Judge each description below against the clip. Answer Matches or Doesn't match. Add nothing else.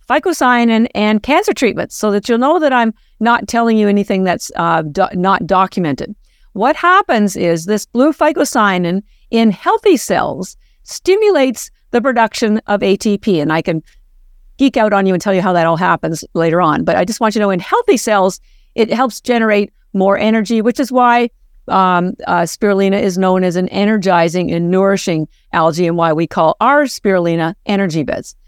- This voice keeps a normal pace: Matches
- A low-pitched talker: Doesn't match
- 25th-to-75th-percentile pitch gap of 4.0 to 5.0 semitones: Matches